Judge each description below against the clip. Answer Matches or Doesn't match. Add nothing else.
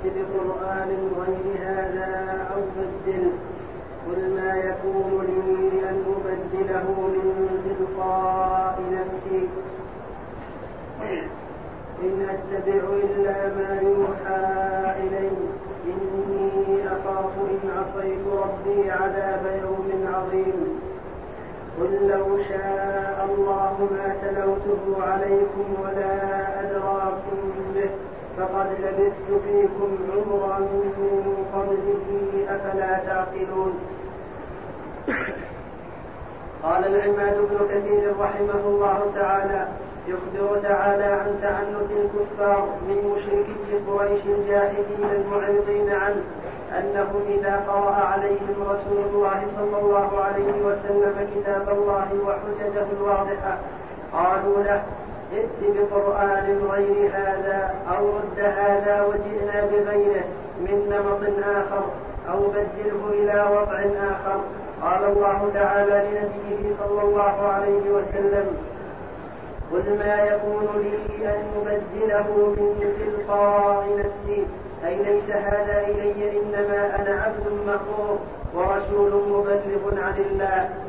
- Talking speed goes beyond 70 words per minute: Matches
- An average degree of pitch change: Doesn't match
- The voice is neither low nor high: Doesn't match